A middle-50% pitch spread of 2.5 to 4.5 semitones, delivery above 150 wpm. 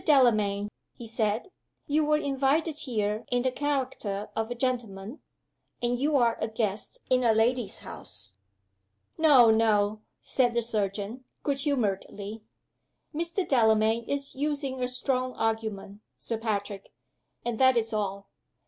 No: average, 3.9 semitones; slow, 135 wpm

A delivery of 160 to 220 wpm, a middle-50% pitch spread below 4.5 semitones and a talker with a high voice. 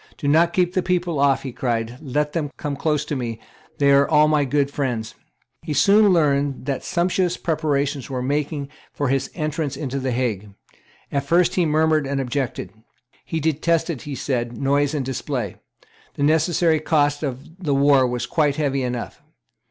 No: average, 175 wpm; average, 2.9 semitones; medium, 145 Hz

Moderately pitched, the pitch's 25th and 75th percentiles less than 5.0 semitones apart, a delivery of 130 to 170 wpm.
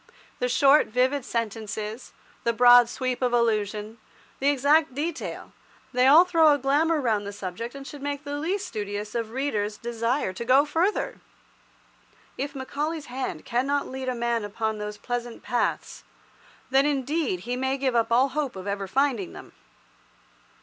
No: very high, 250 Hz; average, 4.2 semitones; average, 160 wpm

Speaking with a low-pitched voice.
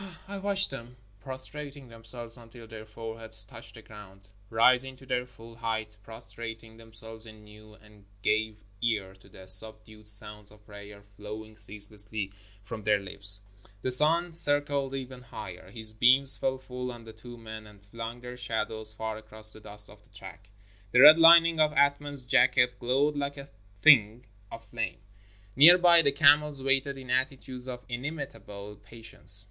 Yes: low, 115 Hz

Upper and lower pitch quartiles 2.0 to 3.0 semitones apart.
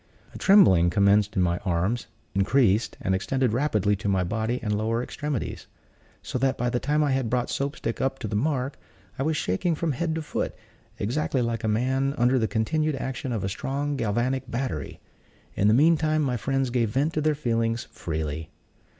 No: average, 4.8 semitones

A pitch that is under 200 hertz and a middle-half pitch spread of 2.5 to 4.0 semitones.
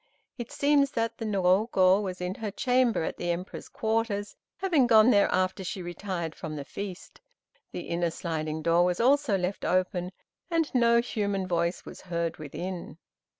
No: high, 190 Hz; average, 4.6 semitones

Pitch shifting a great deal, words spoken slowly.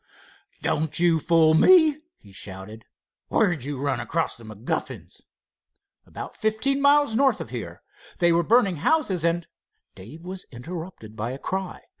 No: wide, 8.7 semitones; average, 150 wpm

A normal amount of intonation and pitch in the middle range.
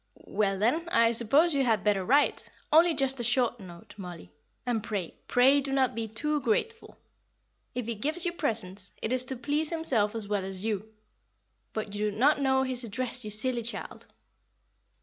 No: average, 4.5 semitones; high, 235 Hz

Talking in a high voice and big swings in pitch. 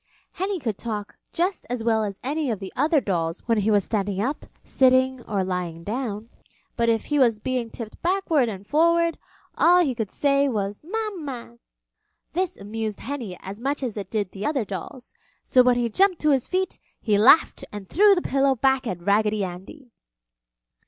Yes: high, 240 Hz; wide, 5.8 semitones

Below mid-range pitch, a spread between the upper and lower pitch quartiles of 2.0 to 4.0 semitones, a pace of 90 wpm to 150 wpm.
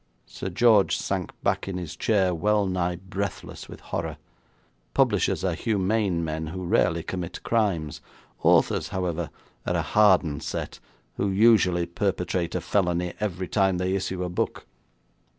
Yes: very low, 90 Hz; narrow, 2.4 semitones; average, 140 wpm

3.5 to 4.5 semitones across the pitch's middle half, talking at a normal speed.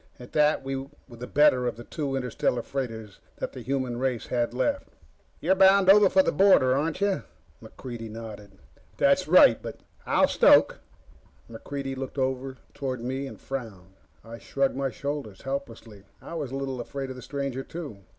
No: average, 2.7 semitones; average, 170 wpm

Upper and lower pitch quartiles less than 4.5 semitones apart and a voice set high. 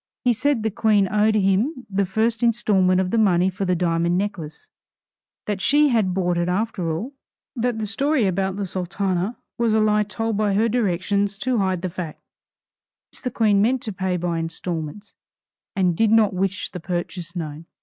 Yes: average, 3.6 semitones; high, 200 Hz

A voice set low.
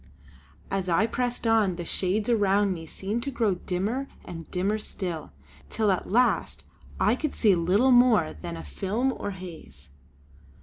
No: high, 195 Hz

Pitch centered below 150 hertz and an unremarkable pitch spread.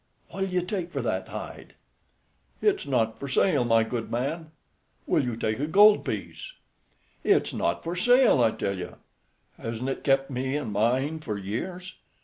No: low, 135 Hz; wide, 7.3 semitones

